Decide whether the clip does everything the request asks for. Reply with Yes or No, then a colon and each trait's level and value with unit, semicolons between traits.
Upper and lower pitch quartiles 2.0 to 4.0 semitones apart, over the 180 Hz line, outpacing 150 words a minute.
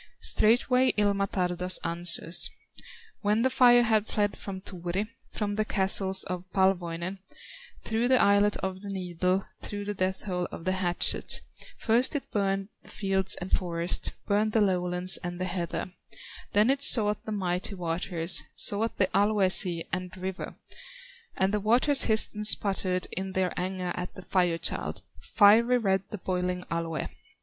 Yes: narrow, 2.5 semitones; high, 190 Hz; average, 160 wpm